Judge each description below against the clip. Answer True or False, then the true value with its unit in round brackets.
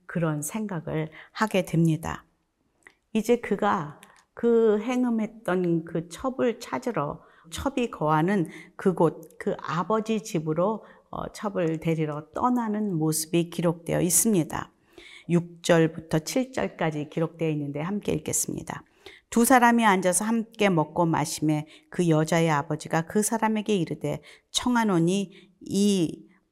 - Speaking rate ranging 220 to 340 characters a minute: True (255 characters per minute)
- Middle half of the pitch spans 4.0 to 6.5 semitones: True (5.2 semitones)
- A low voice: False (180 Hz)